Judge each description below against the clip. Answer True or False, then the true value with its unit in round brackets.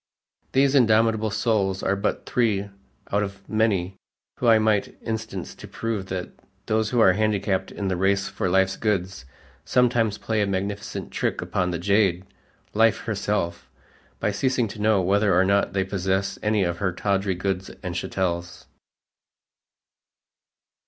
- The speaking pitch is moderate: False (100 Hz)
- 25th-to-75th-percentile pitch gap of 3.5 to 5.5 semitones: False (2.4 semitones)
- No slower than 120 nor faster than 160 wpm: True (150 wpm)